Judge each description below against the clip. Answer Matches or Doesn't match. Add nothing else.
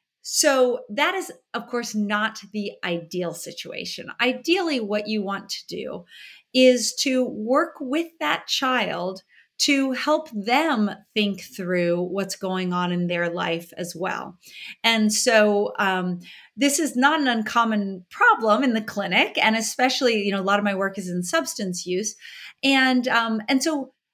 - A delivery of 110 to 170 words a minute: Matches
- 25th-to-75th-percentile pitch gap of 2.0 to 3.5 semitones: Doesn't match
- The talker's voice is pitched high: Matches